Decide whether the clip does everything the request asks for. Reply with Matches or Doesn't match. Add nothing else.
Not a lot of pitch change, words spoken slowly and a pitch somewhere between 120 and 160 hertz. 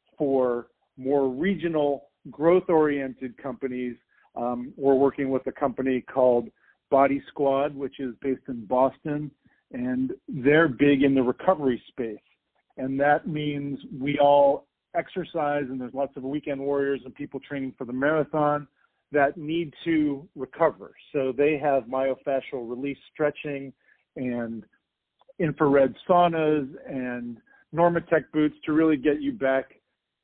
Matches